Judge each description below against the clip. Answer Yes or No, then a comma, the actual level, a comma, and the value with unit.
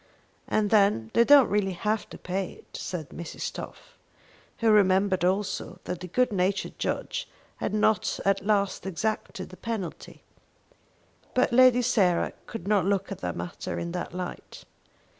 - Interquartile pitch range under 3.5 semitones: Yes, average, 2.9 semitones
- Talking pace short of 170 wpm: Yes, average, 155 wpm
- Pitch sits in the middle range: No, high, 195 Hz